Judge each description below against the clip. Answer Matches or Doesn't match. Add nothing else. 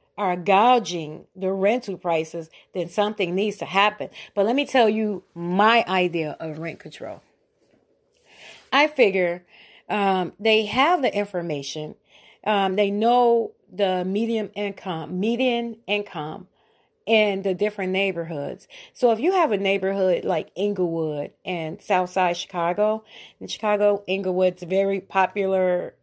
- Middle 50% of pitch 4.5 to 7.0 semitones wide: Doesn't match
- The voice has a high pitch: Matches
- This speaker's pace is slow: Matches